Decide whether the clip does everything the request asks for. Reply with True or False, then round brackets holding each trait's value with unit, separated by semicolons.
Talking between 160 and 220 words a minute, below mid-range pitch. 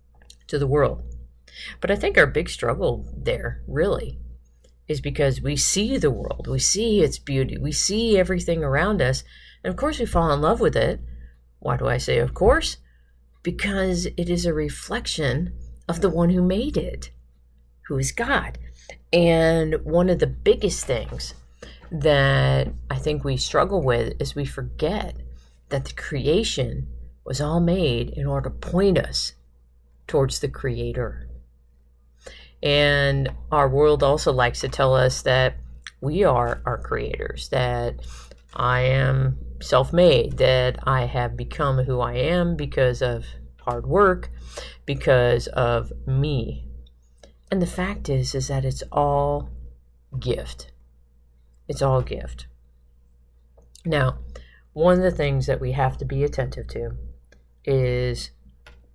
False (145 wpm; 125 Hz)